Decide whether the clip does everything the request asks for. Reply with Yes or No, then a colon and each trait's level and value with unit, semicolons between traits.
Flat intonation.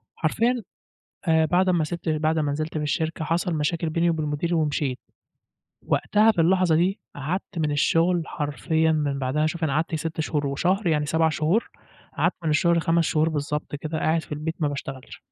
Yes: narrow, 2.2 semitones